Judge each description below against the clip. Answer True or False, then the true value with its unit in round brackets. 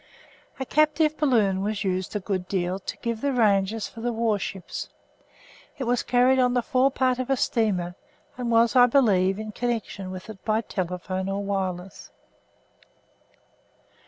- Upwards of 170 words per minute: False (155 wpm)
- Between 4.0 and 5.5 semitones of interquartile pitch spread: True (4.4 semitones)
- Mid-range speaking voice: False (220 Hz)